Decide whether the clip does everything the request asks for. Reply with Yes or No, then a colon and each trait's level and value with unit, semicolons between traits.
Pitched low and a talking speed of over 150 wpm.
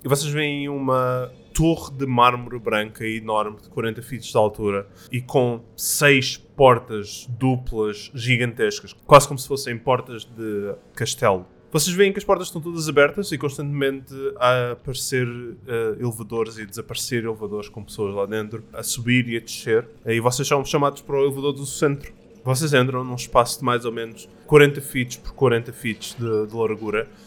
Yes: low, 125 Hz; average, 170 wpm